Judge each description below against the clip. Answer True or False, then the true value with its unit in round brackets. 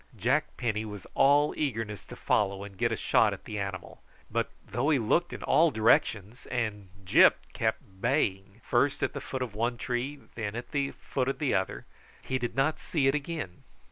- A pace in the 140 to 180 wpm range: False (190 wpm)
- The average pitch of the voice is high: False (120 Hz)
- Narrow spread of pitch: False (5.0 semitones)